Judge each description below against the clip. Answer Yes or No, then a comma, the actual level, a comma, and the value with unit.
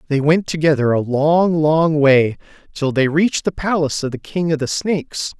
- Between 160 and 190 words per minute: No, average, 200 wpm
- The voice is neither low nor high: Yes, medium, 150 Hz